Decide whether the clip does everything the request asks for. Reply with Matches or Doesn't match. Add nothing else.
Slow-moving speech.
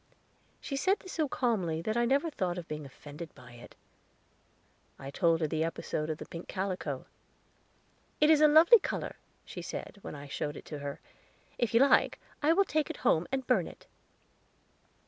Doesn't match